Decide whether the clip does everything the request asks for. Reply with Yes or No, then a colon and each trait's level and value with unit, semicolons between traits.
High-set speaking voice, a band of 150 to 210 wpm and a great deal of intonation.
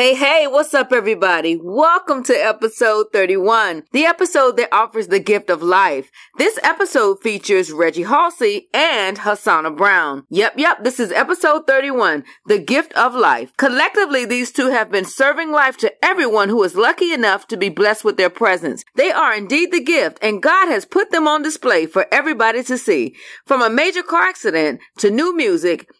Yes: very high, 255 Hz; average, 180 wpm; wide, 7.5 semitones